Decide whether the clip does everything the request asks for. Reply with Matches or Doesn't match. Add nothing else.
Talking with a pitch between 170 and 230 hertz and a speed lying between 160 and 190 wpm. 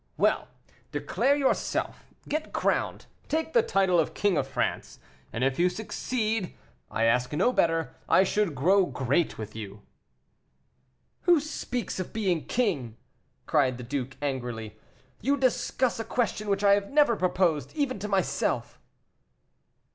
Doesn't match